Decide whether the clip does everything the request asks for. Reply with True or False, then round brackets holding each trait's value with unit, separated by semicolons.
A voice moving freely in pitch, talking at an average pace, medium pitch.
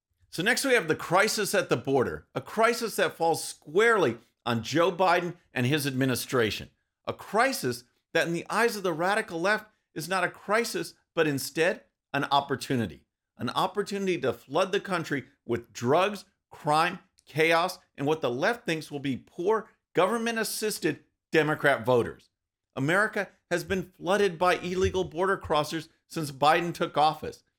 True (5.7 semitones; 155 wpm; 170 Hz)